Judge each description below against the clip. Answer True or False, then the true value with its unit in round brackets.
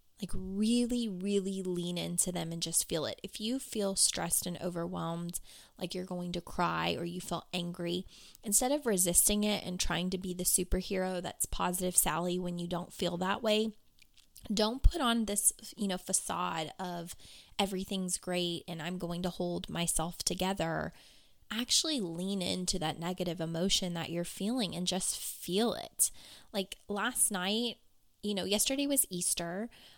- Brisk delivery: False (165 wpm)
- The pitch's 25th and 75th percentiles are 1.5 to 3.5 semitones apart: True (2.9 semitones)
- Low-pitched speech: False (185 Hz)